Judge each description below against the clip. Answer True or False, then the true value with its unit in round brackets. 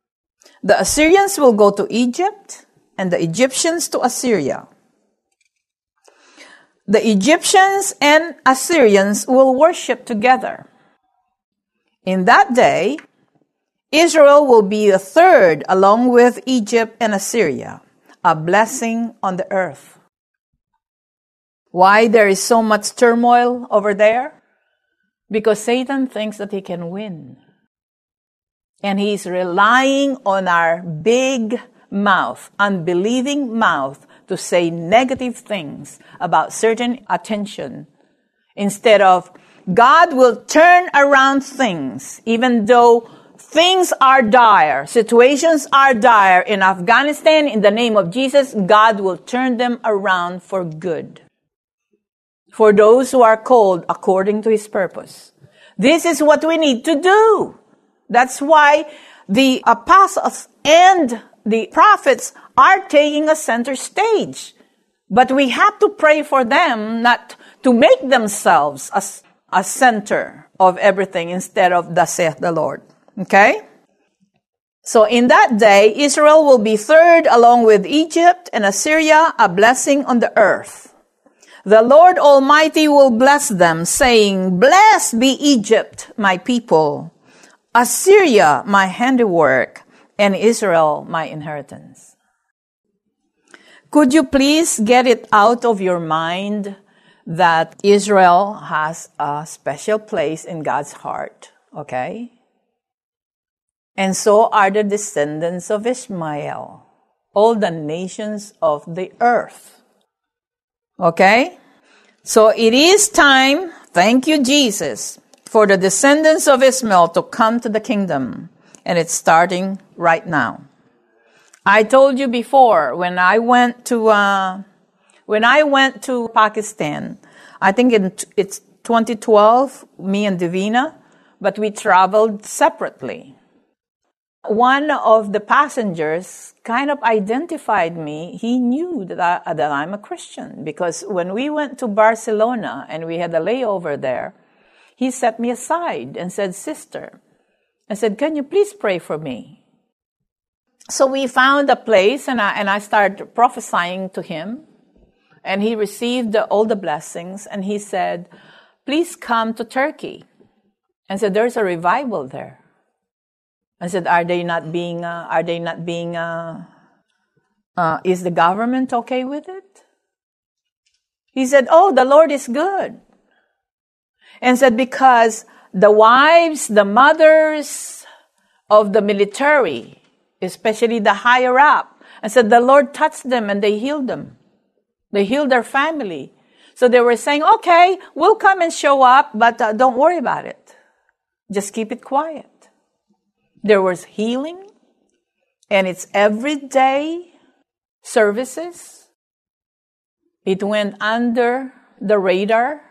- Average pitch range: False (5.7 semitones)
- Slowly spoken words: True (125 wpm)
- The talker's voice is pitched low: False (230 Hz)